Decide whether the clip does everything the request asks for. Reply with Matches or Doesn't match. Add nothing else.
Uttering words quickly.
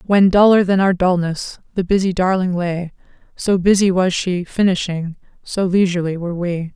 Doesn't match